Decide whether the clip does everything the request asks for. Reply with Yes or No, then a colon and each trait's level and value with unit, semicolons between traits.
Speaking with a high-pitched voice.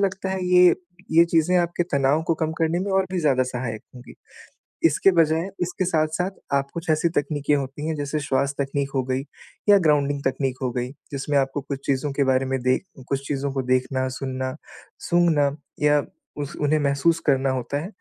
No: medium, 145 Hz